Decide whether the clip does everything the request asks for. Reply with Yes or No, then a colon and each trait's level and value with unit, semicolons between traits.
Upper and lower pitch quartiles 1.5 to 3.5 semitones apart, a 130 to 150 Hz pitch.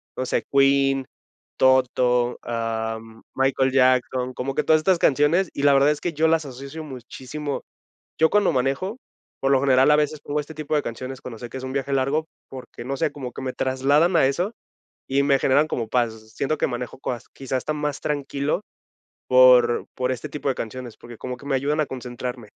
Yes: narrow, 2.6 semitones; low, 135 Hz